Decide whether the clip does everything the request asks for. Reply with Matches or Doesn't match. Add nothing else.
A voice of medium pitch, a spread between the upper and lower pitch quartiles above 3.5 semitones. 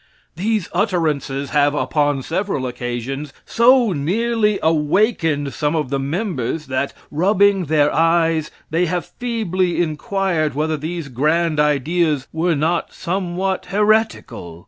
Matches